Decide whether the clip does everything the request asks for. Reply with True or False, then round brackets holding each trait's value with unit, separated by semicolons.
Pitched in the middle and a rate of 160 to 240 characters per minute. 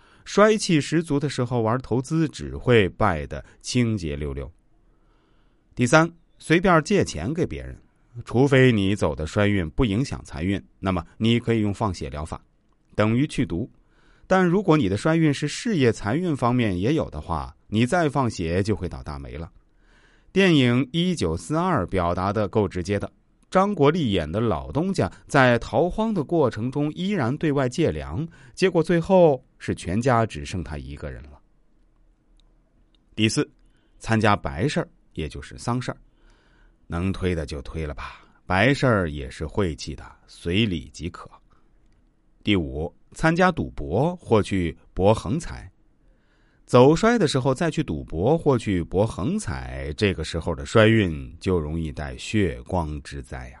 False (110 Hz; 225 characters per minute)